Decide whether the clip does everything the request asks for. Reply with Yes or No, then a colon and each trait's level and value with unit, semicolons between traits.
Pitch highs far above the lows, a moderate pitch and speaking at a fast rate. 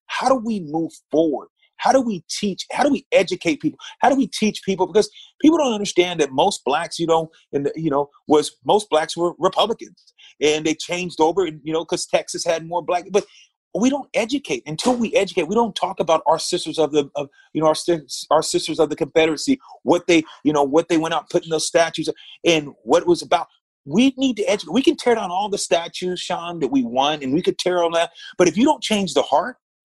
Yes: wide, 5.9 semitones; medium, 175 Hz; fast, 235 wpm